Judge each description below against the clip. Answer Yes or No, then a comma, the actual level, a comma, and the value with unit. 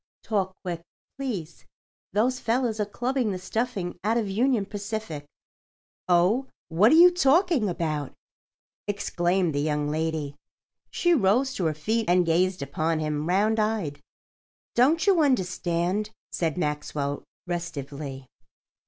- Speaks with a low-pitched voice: No, high, 190 Hz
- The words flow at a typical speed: No, slow, 125 wpm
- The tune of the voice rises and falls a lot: Yes, wide, 6.1 semitones